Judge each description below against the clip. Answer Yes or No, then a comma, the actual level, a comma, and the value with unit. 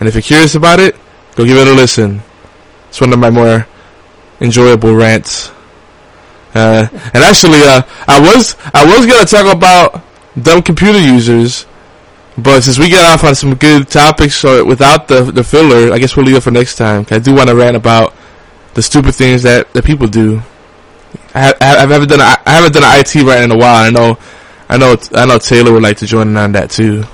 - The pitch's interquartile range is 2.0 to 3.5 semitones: No, average, 4.7 semitones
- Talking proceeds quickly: Yes, fast, 210 wpm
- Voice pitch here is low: Yes, low, 120 Hz